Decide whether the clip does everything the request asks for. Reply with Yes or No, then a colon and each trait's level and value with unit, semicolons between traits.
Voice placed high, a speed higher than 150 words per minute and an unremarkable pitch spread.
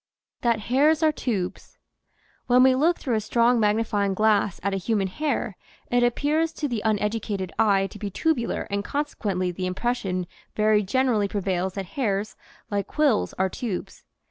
Yes: high, 215 Hz; average, 165 wpm; average, 4.1 semitones